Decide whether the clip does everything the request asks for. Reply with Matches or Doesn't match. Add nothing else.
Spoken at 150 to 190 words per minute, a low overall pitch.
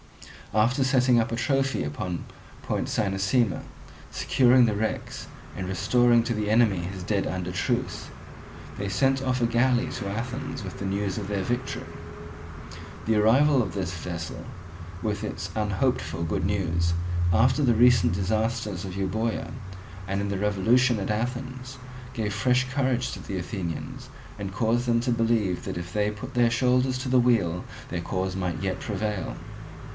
Matches